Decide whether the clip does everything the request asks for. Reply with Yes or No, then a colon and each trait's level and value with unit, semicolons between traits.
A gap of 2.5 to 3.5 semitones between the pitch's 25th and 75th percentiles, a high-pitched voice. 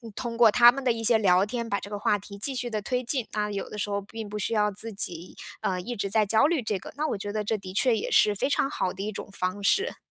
Yes: average, 2.9 semitones; high, 215 Hz